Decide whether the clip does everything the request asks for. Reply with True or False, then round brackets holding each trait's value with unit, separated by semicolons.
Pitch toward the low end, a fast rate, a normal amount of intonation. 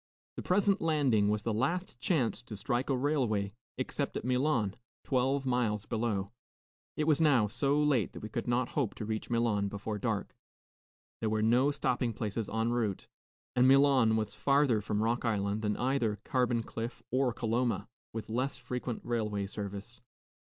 False (120 Hz; 165 wpm; 3.5 semitones)